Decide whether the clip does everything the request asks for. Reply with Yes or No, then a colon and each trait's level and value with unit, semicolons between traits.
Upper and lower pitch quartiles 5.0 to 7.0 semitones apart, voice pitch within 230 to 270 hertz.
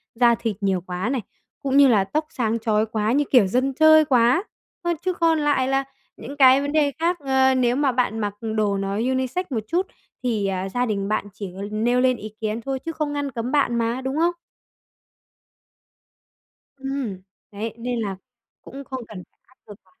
No: average, 4.4 semitones; very high, 250 Hz